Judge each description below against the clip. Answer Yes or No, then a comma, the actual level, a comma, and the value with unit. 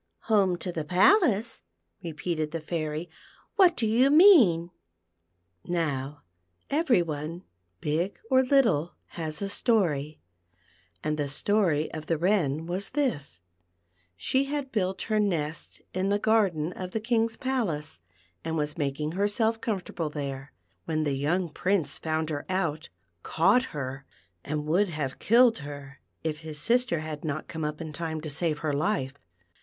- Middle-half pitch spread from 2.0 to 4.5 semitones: No, wide, 5.5 semitones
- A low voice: No, medium, 165 Hz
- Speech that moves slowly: No, average, 165 wpm